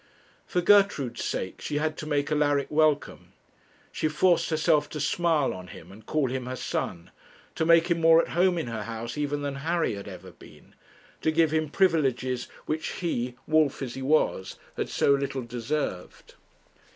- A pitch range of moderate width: Yes, average, 4.1 semitones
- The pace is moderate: Yes, average, 175 wpm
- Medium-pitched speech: Yes, medium, 145 Hz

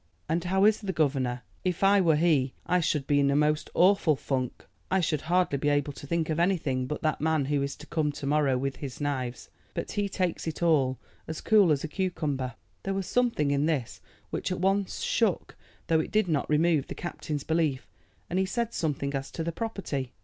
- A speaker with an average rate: No, fast, 215 wpm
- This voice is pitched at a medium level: Yes, medium, 155 Hz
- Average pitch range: Yes, average, 4.3 semitones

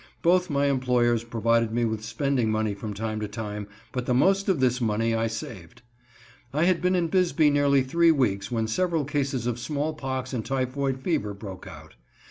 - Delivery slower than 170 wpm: No, average, 185 wpm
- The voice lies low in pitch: Yes, low, 125 Hz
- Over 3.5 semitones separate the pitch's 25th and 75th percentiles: Yes, average, 4.5 semitones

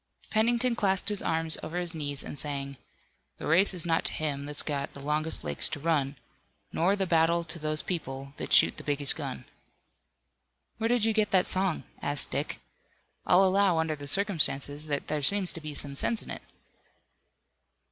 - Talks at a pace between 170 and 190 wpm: Yes, average, 185 wpm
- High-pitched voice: No, medium, 160 Hz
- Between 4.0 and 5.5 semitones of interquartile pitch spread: Yes, average, 4.8 semitones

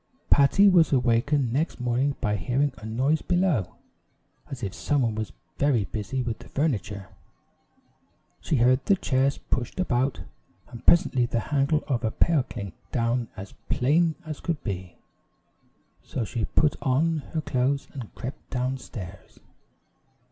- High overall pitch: No, low, 130 Hz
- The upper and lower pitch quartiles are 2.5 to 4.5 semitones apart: Yes, average, 4.1 semitones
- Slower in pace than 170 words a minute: Yes, average, 145 wpm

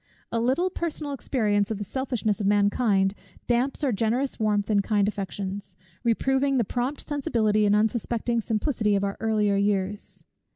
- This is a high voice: Yes, high, 220 Hz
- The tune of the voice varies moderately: Yes, average, 3.7 semitones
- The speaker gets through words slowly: No, average, 155 wpm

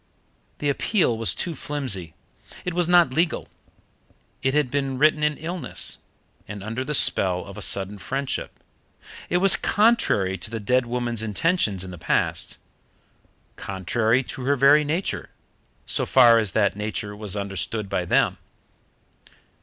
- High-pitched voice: No, low, 125 Hz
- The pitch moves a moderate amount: No, wide, 6.6 semitones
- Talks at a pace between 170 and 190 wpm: No, average, 145 wpm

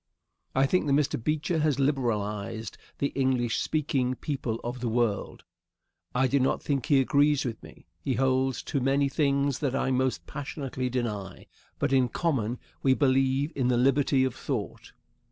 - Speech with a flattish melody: Yes, narrow, 2.3 semitones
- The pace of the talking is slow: No, average, 165 wpm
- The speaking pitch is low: Yes, low, 130 Hz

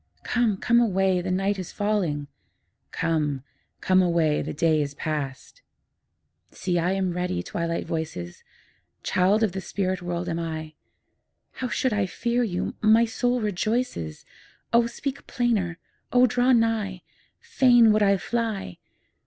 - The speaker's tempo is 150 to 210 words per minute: No, average, 140 wpm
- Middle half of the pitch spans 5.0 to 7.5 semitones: Yes, wide, 5.4 semitones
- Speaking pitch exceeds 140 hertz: Yes, high, 190 Hz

